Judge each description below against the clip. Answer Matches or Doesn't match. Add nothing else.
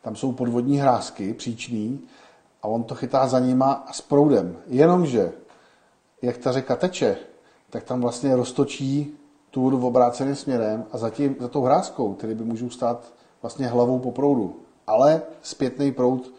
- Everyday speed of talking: Matches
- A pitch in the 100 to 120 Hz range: Doesn't match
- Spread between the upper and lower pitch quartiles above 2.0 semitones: Matches